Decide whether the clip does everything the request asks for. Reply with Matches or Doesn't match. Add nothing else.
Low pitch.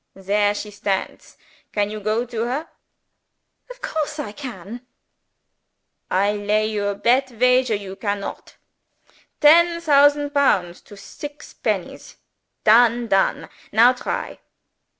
Doesn't match